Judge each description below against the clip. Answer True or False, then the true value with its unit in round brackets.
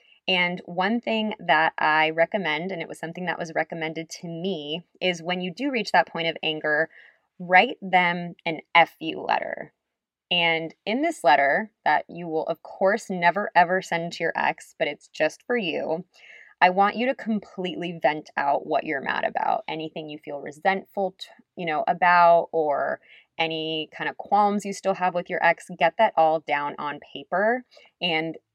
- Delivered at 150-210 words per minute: True (185 wpm)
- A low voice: False (175 Hz)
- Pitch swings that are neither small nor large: True (3.2 semitones)